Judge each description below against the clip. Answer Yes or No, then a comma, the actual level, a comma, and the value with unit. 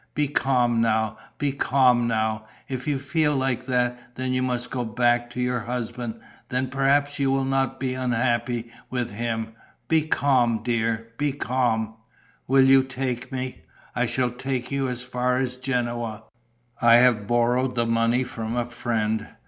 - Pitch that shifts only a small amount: Yes, narrow, 2.0 semitones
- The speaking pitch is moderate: No, low, 125 Hz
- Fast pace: No, average, 165 wpm